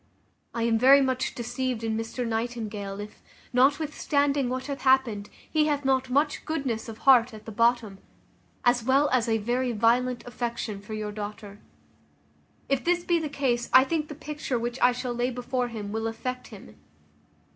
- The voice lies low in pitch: No, high, 245 Hz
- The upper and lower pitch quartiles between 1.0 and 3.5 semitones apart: Yes, average, 2.9 semitones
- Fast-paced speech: No, average, 175 wpm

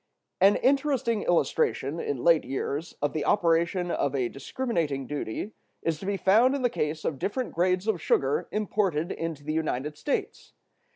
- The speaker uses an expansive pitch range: Yes, wide, 5.8 semitones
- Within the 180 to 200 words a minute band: No, average, 165 wpm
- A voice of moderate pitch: Yes, medium, 170 Hz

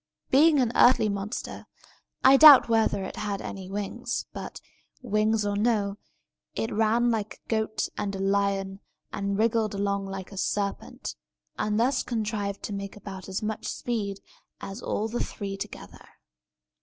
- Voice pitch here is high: Yes, high, 210 Hz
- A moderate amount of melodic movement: No, narrow, 2.1 semitones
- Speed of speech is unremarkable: Yes, average, 155 wpm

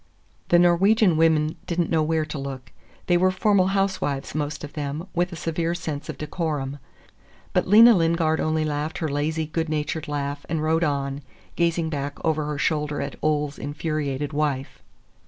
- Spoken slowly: No, average, 175 wpm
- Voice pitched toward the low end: No, medium, 155 Hz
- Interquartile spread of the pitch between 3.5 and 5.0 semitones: No, narrow, 2.4 semitones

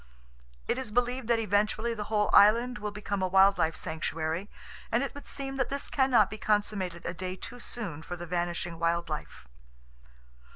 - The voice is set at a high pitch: Yes, high, 205 Hz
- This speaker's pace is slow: No, average, 190 wpm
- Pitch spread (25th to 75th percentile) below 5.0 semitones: No, average, 5.3 semitones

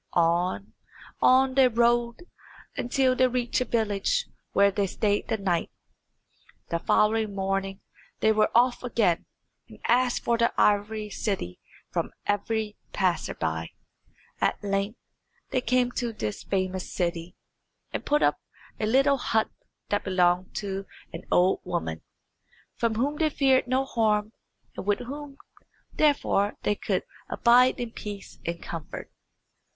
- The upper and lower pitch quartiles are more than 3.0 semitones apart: Yes, average, 4.3 semitones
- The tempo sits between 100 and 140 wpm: Yes, slow, 135 wpm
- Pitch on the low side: No, high, 215 Hz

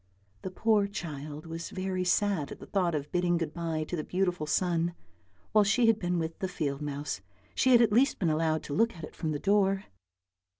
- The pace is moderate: No, fast, 215 wpm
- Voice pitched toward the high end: No, medium, 175 Hz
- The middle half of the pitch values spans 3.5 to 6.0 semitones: Yes, average, 4.0 semitones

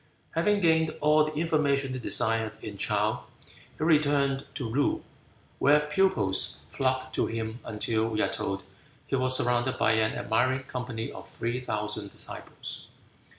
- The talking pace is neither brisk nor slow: Yes, average, 150 wpm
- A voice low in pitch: Yes, low, 130 Hz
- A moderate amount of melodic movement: Yes, average, 4.8 semitones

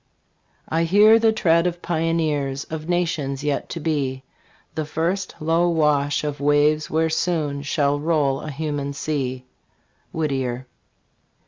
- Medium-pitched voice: Yes, medium, 155 Hz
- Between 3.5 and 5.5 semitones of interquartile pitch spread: No, narrow, 2.6 semitones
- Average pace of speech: No, slow, 130 wpm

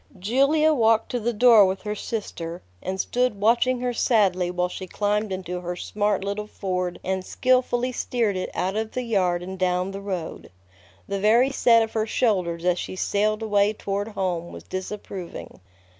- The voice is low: No, high, 205 Hz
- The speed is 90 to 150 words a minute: No, average, 175 wpm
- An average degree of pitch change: Yes, average, 3.5 semitones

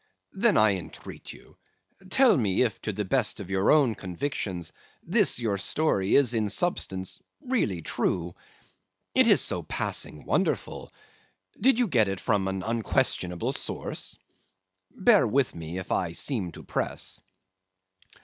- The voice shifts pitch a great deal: Yes, wide, 6.2 semitones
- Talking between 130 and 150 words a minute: Yes, average, 140 wpm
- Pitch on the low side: Yes, low, 105 Hz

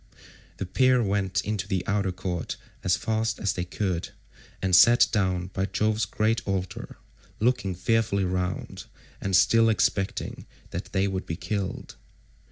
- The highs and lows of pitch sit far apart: No, average, 2.8 semitones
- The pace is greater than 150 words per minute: No, average, 145 wpm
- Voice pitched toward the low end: Yes, very low, 95 Hz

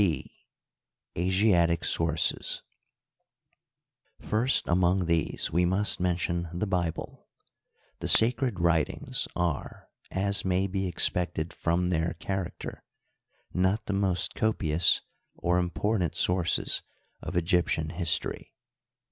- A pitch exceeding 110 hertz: No, very low, 90 Hz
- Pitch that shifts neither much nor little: No, narrow, 2.2 semitones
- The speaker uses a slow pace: Yes, slow, 105 wpm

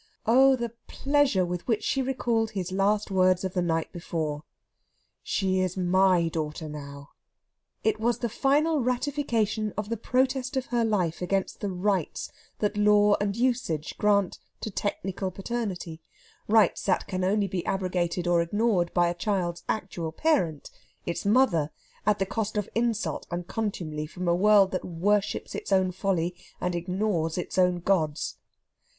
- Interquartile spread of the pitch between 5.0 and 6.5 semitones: No, average, 3.9 semitones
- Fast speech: No, average, 155 wpm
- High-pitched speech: Yes, high, 195 Hz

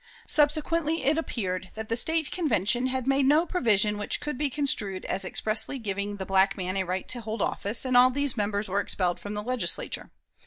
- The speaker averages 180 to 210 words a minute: Yes, average, 200 wpm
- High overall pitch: Yes, high, 225 Hz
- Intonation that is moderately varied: No, wide, 5.8 semitones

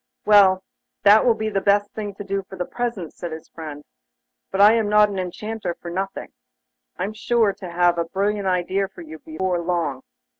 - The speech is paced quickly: No, average, 195 wpm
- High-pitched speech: Yes, high, 195 Hz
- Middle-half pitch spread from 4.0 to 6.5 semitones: No, average, 3.0 semitones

